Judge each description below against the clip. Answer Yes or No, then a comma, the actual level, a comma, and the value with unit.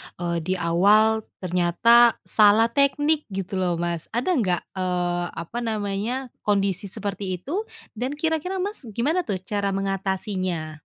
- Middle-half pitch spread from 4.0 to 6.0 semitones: Yes, average, 4.7 semitones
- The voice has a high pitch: Yes, high, 200 Hz